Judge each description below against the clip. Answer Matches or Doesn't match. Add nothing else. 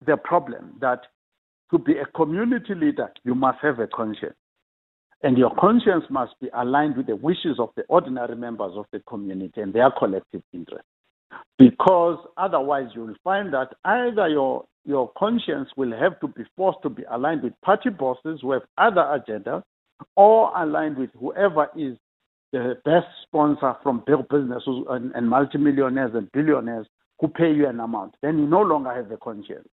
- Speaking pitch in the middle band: Matches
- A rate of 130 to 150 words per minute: Doesn't match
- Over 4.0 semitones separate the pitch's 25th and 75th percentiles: Matches